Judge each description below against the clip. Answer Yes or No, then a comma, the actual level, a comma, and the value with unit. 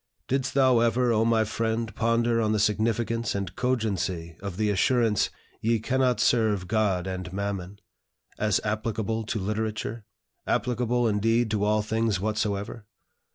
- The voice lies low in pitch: Yes, low, 110 Hz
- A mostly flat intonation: Yes, narrow, 2.1 semitones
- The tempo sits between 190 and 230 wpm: No, average, 140 wpm